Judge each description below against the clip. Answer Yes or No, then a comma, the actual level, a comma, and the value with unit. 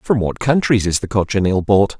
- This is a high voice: No, low, 105 Hz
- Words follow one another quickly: Yes, fast, 210 wpm